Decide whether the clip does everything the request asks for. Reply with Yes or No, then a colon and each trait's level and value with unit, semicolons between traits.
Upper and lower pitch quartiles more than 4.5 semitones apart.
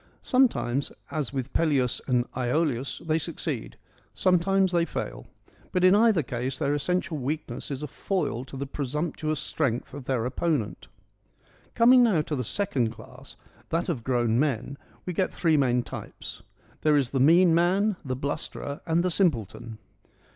Yes: average, 5.2 semitones